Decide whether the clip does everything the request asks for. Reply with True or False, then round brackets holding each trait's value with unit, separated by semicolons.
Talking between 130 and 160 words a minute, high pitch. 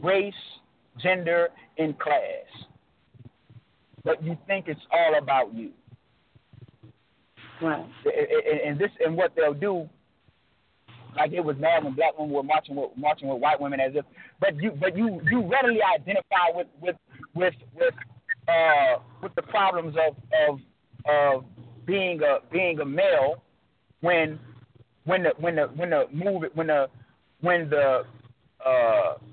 False (140 wpm; 170 Hz)